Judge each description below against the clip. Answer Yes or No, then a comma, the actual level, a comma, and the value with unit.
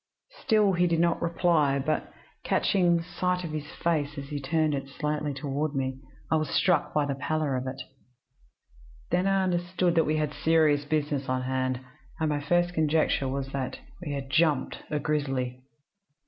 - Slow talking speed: No, average, 175 wpm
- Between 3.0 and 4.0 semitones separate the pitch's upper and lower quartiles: Yes, average, 3.3 semitones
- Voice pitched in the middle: Yes, medium, 150 Hz